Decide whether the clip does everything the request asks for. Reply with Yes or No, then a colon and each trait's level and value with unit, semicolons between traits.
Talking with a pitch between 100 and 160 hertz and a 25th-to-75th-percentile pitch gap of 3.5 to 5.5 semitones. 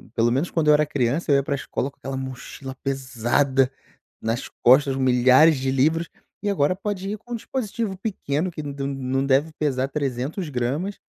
Yes: medium, 140 Hz; average, 3.8 semitones